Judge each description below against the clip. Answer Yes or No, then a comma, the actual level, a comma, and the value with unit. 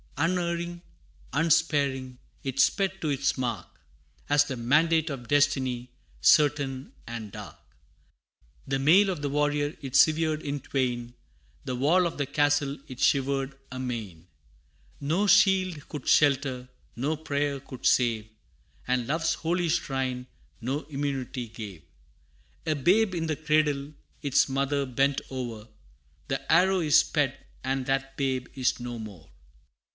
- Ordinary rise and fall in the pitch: Yes, average, 3.3 semitones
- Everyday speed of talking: No, slow, 130 wpm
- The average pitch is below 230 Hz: Yes, medium, 140 Hz